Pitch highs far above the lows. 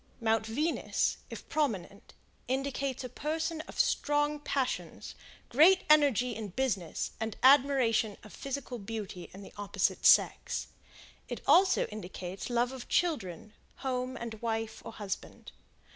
No: average, 4.7 semitones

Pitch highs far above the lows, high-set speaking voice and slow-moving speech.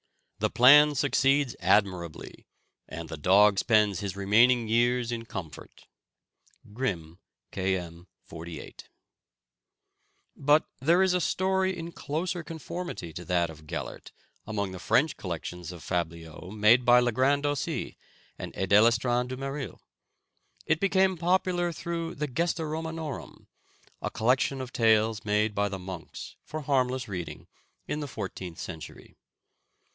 No: wide, 7.9 semitones; low, 120 Hz; slow, 130 wpm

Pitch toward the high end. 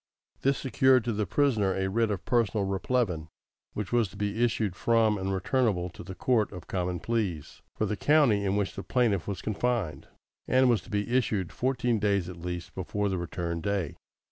No: low, 105 Hz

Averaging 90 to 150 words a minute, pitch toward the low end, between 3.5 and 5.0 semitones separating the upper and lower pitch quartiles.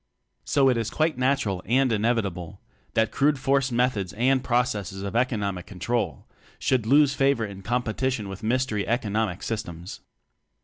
Yes: average, 145 wpm; low, 115 Hz; average, 4.3 semitones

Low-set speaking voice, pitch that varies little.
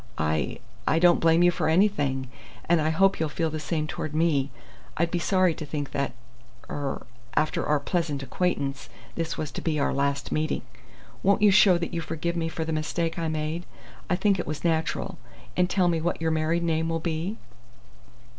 No: medium, 160 Hz; narrow, 2.2 semitones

